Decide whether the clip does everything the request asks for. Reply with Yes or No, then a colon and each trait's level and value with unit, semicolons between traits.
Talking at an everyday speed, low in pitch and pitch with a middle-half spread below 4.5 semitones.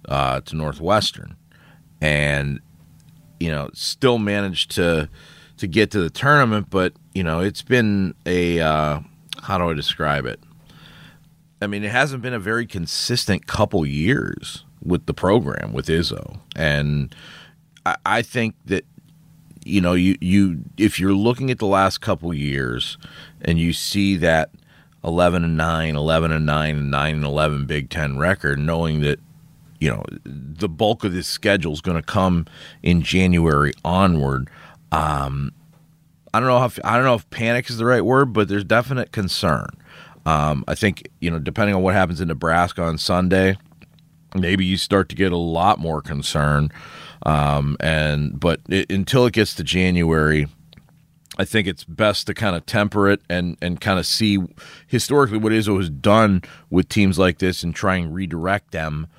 No: average, 170 wpm; very low, 90 Hz; average, 5.0 semitones